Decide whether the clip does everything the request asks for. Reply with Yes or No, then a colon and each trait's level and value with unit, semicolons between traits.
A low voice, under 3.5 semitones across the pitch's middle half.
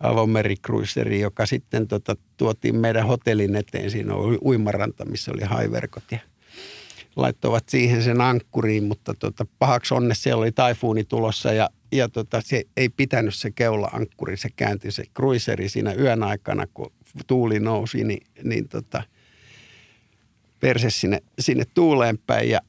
Yes: low, 115 Hz; average, 2.8 semitones